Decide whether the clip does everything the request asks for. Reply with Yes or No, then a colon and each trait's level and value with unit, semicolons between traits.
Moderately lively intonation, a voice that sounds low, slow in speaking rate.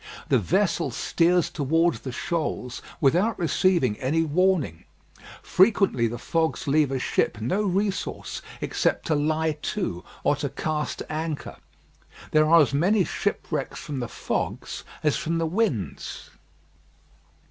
No: average, 4.0 semitones; medium, 155 Hz; slow, 130 wpm